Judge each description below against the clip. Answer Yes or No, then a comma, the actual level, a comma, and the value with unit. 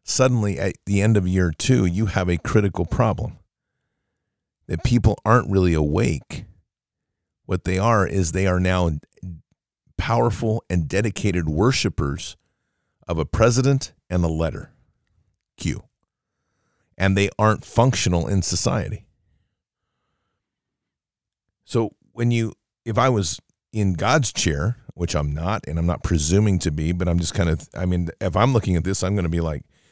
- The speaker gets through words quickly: No, average, 150 wpm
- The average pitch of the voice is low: Yes, very low, 95 Hz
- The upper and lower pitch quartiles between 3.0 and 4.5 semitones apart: Yes, average, 4.2 semitones